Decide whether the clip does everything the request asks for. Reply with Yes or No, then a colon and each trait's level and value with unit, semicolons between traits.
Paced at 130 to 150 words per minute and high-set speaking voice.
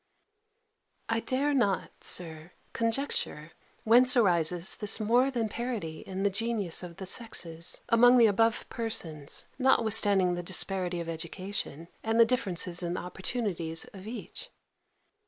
Yes: slow, 135 wpm; high, 200 Hz